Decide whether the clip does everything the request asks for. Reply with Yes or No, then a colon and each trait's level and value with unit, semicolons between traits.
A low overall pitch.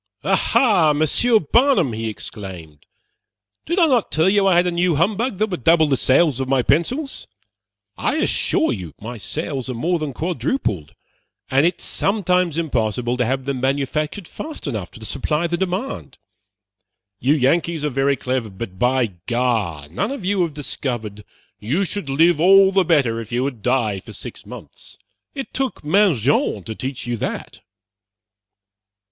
No: medium, 145 Hz